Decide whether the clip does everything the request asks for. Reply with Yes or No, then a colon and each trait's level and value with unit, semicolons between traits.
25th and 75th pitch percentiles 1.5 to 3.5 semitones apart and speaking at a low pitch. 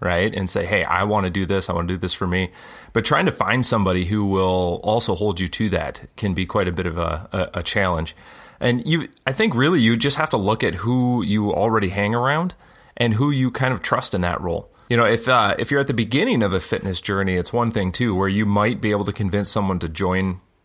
No: average, 4.2 semitones; low, 100 Hz